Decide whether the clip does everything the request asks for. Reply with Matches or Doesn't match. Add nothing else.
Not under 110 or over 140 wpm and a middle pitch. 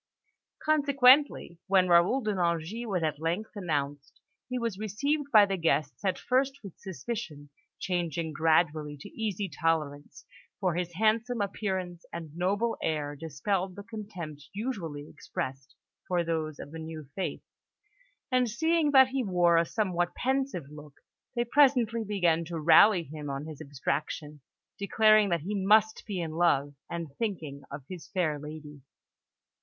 Doesn't match